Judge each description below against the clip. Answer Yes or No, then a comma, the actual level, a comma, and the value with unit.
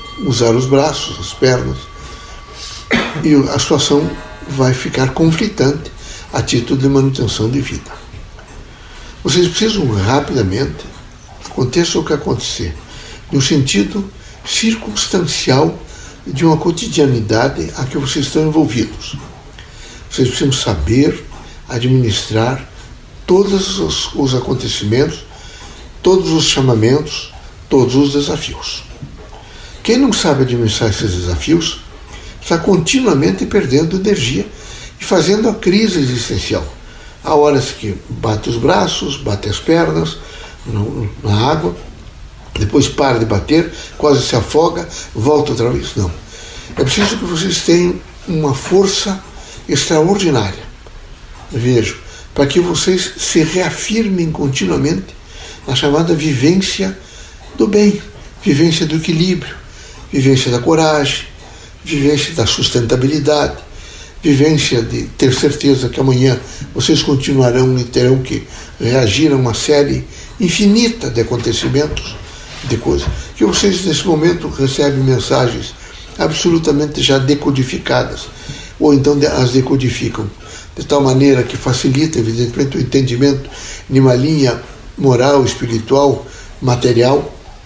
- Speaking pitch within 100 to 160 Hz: Yes, low, 135 Hz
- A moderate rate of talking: No, slow, 110 wpm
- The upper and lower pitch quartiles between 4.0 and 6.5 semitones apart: Yes, average, 5.1 semitones